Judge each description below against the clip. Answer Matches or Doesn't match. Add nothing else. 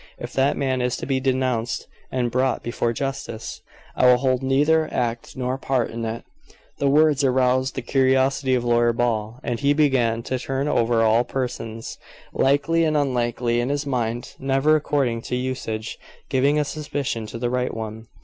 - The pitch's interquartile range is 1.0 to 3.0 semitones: Matches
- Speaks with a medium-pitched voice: Doesn't match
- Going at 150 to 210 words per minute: Matches